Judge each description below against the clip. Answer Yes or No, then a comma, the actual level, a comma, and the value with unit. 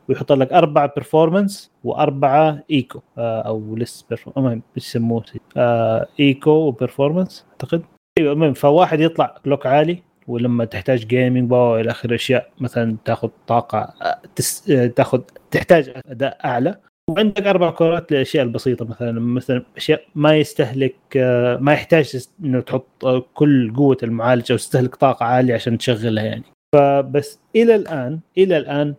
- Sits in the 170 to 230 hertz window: No, low, 135 Hz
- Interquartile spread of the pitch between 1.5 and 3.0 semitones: No, average, 3.9 semitones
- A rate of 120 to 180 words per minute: Yes, average, 130 wpm